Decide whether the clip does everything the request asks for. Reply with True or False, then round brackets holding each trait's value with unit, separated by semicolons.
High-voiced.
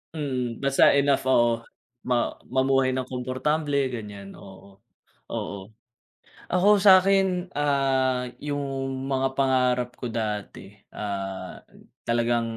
False (130 Hz)